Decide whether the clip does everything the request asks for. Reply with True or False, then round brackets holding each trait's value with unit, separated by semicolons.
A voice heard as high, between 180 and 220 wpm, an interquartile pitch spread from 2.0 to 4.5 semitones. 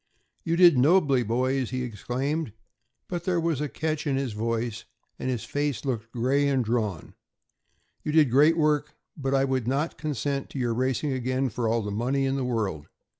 False (130 Hz; 185 wpm; 3.7 semitones)